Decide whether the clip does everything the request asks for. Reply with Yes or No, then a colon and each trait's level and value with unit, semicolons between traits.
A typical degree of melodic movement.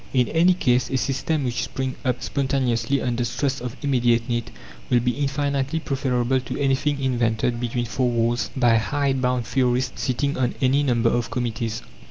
No: narrow, 2.2 semitones